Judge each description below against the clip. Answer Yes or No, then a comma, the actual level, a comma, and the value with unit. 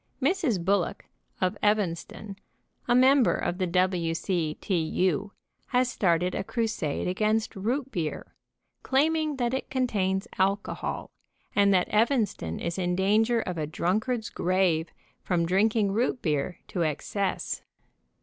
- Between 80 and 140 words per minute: Yes, slow, 135 wpm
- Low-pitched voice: No, high, 195 Hz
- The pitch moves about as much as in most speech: Yes, average, 4.6 semitones